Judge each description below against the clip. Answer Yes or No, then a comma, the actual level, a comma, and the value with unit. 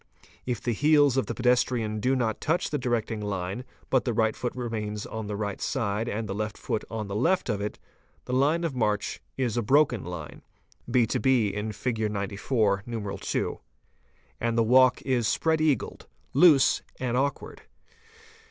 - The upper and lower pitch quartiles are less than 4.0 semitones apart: Yes, average, 3.5 semitones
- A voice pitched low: Yes, low, 115 Hz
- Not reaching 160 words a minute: No, average, 165 wpm